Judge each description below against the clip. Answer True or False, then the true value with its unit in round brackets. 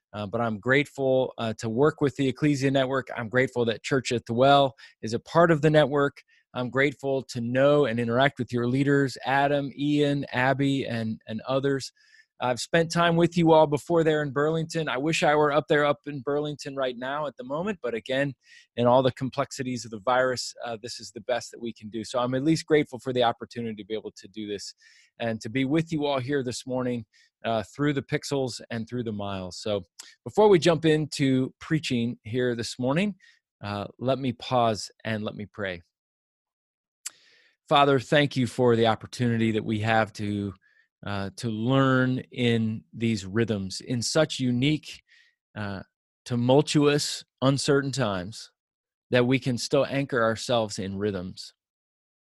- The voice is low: True (130 Hz)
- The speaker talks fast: False (185 wpm)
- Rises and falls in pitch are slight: False (4.0 semitones)